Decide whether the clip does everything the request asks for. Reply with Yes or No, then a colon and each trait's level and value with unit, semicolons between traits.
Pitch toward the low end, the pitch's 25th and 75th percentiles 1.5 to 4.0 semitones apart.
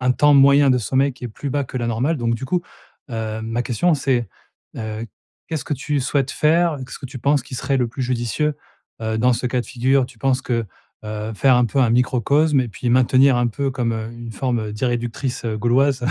Yes: low, 125 Hz; average, 2.8 semitones